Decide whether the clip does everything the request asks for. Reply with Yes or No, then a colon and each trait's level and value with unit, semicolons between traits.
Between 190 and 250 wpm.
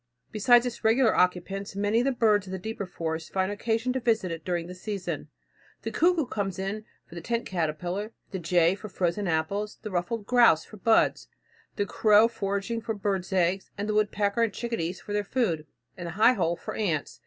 Yes: average, 195 wpm